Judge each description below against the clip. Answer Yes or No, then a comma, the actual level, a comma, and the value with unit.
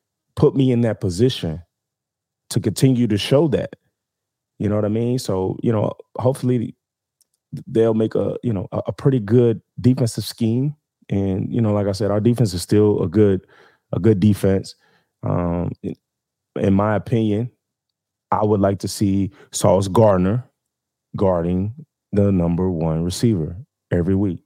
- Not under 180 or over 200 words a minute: No, average, 150 wpm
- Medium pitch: No, low, 105 Hz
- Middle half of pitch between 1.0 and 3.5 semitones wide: No, average, 4.1 semitones